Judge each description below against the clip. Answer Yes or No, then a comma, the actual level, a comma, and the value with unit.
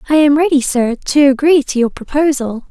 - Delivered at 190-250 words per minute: Yes, average, 200 wpm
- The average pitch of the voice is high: Yes, very high, 280 Hz